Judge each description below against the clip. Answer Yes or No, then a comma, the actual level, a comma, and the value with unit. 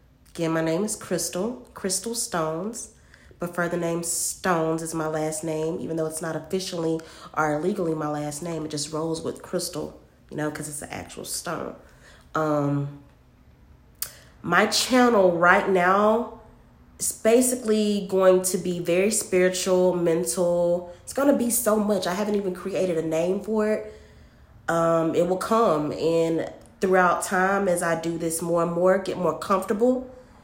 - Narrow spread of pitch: No, average, 3.4 semitones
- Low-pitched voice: No, medium, 175 Hz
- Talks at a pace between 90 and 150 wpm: No, average, 160 wpm